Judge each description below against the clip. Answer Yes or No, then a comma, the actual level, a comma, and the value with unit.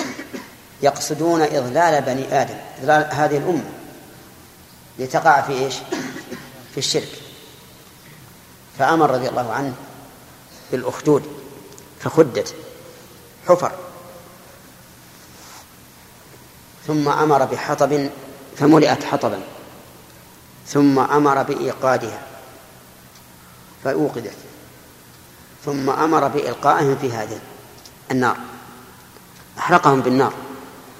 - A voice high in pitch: No, low, 135 Hz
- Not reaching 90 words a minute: Yes, average, 70 wpm